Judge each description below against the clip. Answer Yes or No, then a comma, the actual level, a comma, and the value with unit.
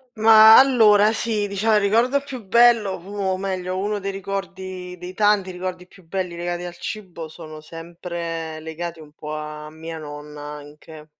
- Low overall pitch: No, medium, 185 Hz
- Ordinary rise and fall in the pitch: Yes, average, 4.0 semitones